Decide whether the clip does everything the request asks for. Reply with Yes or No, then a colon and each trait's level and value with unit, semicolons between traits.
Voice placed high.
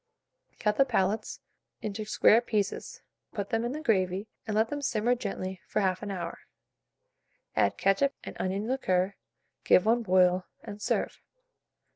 Yes: high, 210 Hz